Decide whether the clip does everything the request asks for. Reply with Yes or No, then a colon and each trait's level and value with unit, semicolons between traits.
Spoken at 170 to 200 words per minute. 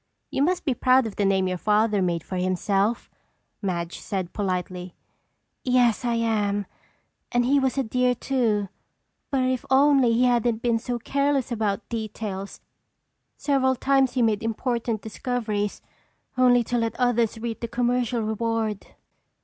No: average, 150 wpm